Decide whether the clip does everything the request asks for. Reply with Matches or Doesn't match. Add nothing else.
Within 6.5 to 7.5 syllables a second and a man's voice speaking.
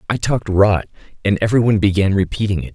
Matches